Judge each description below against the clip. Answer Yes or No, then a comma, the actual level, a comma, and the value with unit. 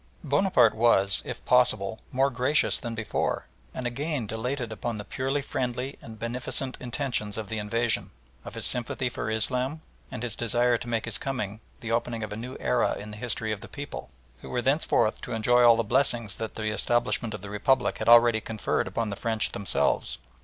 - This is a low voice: Yes, low, 115 Hz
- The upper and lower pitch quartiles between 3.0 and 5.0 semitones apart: No, narrow, 2.6 semitones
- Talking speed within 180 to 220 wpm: Yes, average, 195 wpm